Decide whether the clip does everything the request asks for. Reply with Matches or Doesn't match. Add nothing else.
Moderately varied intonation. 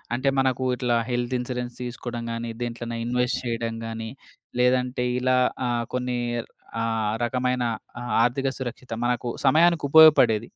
Doesn't match